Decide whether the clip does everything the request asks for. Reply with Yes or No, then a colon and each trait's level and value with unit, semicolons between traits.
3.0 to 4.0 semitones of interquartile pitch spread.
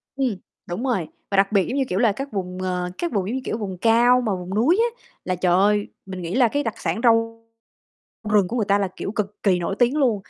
No: average, 4.4 semitones